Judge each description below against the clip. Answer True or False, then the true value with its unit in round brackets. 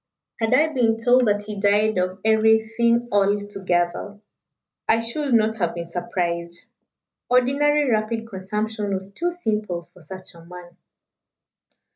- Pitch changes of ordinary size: True (3.7 semitones)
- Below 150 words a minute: True (135 wpm)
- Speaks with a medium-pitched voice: False (210 Hz)